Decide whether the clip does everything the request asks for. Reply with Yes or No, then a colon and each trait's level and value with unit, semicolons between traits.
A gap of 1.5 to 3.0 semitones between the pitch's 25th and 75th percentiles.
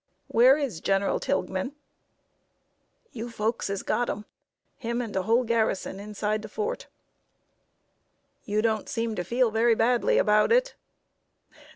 Yes: narrow, 2.5 semitones